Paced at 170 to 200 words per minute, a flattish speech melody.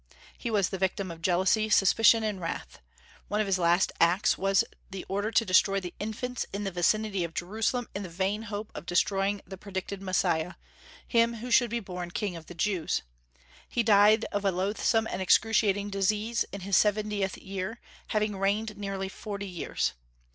Yes: average, 180 wpm; narrow, 2.3 semitones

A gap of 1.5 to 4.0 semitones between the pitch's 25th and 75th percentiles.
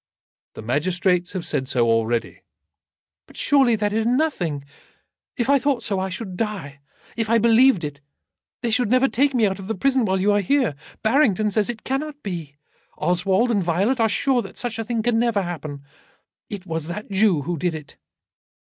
No: wide, 5.5 semitones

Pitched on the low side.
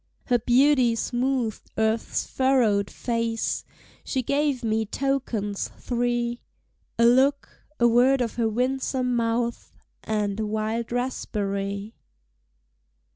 No: high, 235 Hz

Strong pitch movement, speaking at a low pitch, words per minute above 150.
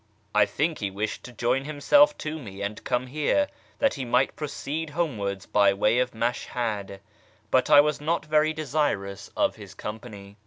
Yes: wide, 6.6 semitones; low, 125 Hz; average, 170 wpm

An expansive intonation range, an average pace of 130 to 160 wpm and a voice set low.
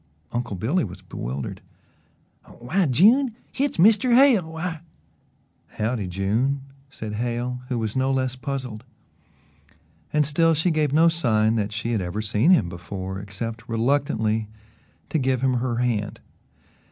Yes: wide, 6.2 semitones; average, 140 wpm; low, 125 Hz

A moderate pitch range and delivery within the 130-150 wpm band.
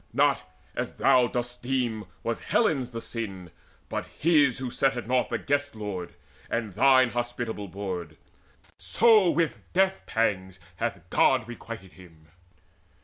Yes: average, 4.8 semitones; average, 140 wpm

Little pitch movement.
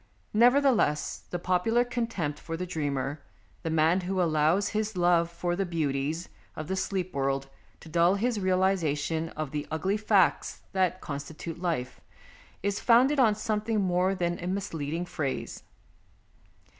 No: average, 4.1 semitones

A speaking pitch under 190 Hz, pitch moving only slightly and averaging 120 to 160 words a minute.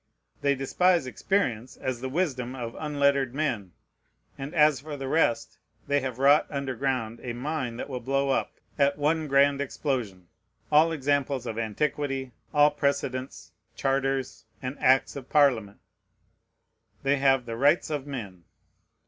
Yes: low, 135 Hz; narrow, 2.3 semitones; average, 145 wpm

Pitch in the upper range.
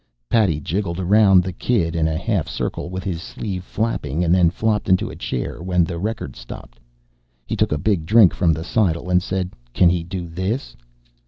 No: very low, 90 Hz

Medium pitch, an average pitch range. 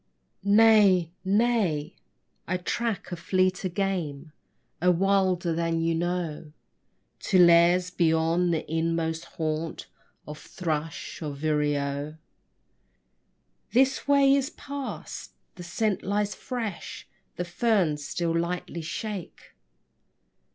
Yes: medium, 175 Hz; average, 3.4 semitones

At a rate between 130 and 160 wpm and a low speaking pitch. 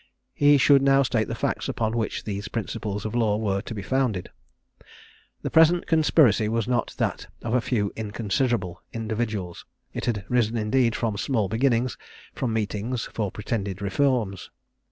Yes: average, 155 wpm; low, 115 Hz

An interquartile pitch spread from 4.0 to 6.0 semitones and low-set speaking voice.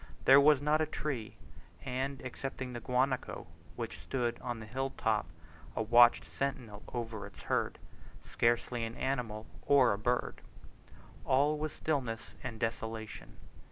No: average, 3.2 semitones; low, 125 Hz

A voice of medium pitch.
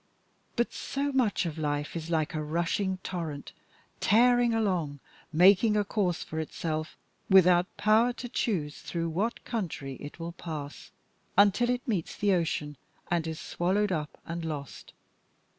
Yes: medium, 175 Hz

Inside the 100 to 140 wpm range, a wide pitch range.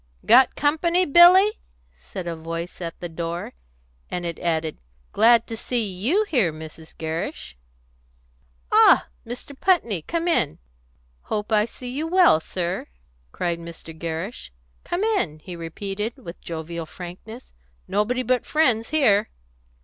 Yes: slow, 135 wpm; wide, 7.6 semitones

